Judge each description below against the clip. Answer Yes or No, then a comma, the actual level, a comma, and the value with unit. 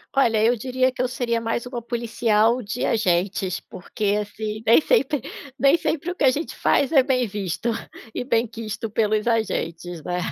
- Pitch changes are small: No, average, 3.3 semitones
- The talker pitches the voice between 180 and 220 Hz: No, high, 230 Hz